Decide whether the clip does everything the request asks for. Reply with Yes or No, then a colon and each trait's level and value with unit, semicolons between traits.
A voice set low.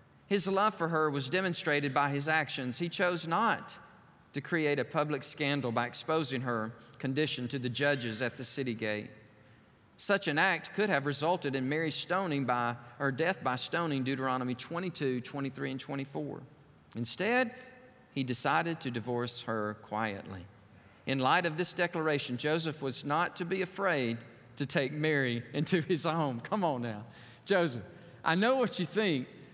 No: medium, 145 Hz